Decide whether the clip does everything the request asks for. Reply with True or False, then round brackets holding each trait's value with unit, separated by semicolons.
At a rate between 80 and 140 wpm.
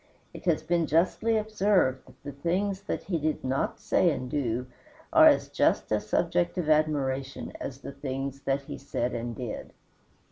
False (175 wpm)